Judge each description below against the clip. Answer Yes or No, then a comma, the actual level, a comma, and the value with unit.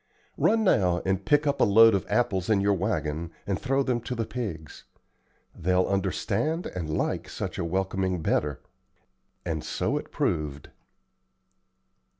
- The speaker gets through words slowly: No, average, 150 wpm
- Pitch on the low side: Yes, very low, 95 Hz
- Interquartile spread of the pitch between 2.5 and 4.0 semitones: No, average, 5.0 semitones